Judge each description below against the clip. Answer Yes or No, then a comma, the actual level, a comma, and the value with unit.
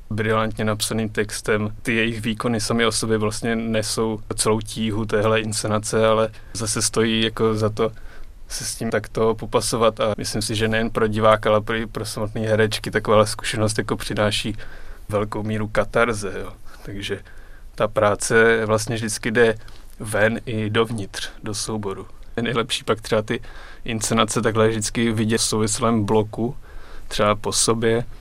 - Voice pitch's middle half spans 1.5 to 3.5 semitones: No, narrow, 1.0 semitones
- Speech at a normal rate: Yes, average, 155 wpm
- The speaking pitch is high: No, low, 110 Hz